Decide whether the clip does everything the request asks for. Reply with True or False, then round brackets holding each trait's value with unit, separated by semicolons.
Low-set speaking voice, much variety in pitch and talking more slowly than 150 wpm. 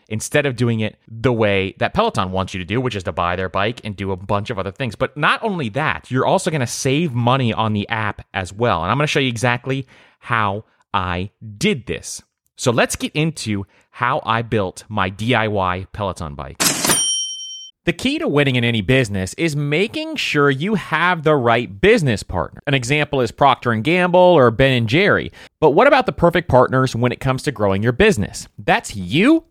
False (120 Hz; 6.4 semitones; 205 wpm)